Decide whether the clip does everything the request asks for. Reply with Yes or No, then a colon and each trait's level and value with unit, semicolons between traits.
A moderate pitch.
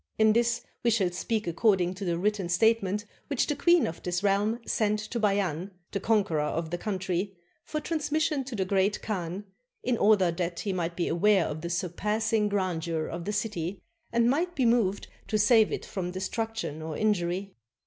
No: high, 200 Hz